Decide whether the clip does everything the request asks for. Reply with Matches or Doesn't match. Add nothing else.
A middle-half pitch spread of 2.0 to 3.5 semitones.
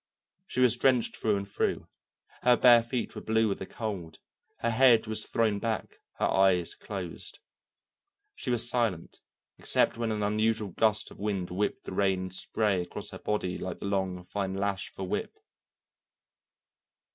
Matches